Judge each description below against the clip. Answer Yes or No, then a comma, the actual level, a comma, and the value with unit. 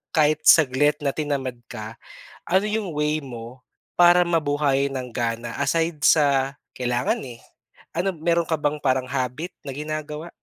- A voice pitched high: No, medium, 145 Hz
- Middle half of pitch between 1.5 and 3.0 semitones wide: No, average, 3.7 semitones